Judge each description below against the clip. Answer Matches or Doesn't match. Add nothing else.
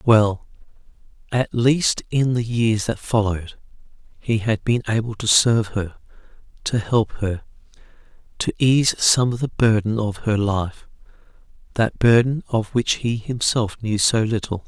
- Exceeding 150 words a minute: Doesn't match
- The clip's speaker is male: Matches